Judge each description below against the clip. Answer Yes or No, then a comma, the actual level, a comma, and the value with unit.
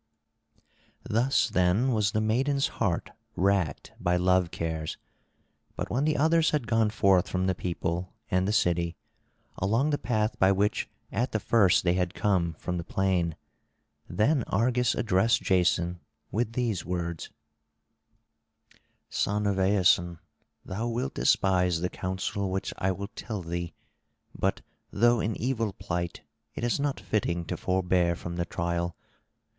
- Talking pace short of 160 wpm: Yes, average, 145 wpm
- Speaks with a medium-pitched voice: No, very low, 95 Hz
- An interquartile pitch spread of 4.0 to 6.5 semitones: Yes, average, 4.3 semitones